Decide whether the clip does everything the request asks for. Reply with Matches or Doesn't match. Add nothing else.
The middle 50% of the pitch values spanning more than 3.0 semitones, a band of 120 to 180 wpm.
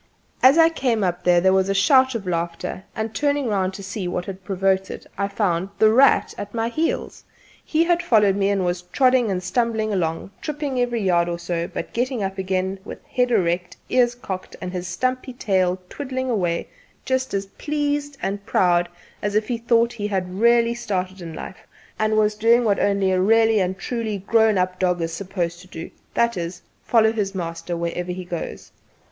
Doesn't match